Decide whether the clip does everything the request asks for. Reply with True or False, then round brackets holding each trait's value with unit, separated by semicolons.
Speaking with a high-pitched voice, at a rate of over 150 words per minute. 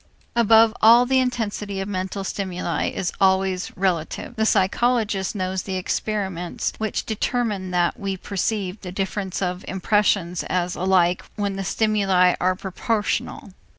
False (195 Hz; 135 wpm)